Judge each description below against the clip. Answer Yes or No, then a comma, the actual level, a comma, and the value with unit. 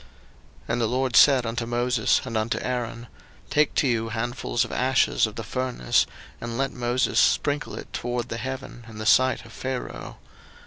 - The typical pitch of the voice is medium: No, low, 120 Hz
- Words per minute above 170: Yes, average, 180 wpm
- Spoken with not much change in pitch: Yes, narrow, 2.0 semitones